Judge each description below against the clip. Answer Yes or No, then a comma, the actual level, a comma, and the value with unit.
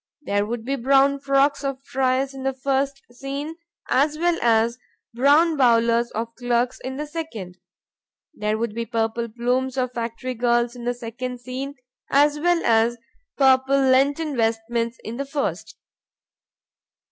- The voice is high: Yes, very high, 255 Hz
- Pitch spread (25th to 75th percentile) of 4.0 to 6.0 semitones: No, average, 2.8 semitones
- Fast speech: No, average, 145 wpm